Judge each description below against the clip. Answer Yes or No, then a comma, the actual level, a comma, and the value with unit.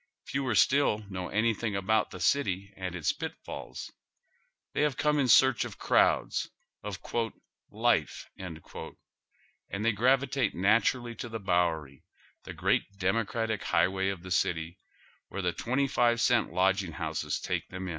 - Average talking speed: Yes, average, 145 wpm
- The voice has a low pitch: Yes, low, 100 Hz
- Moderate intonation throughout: Yes, average, 4.4 semitones